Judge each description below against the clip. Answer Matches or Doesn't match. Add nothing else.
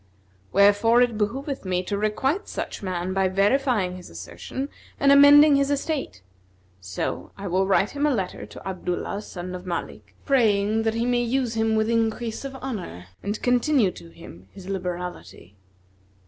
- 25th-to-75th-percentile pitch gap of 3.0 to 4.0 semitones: Doesn't match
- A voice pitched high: Matches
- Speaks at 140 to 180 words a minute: Matches